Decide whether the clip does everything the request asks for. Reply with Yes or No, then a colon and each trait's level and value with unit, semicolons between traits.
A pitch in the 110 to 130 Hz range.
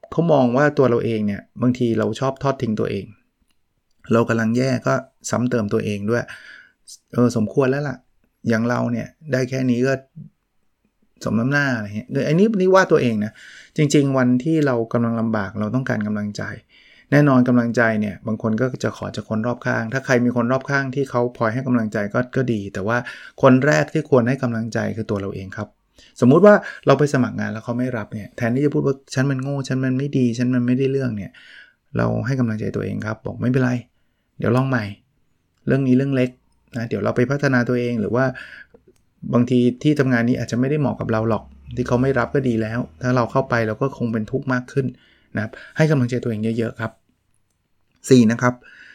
Yes: low, 125 Hz